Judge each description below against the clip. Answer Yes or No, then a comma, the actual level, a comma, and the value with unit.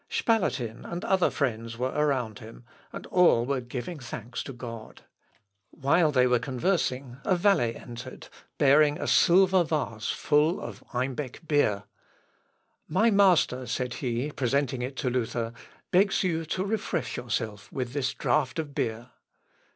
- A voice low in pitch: Yes, low, 130 Hz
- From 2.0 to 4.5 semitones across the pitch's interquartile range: No, average, 5.0 semitones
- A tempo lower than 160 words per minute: Yes, average, 145 wpm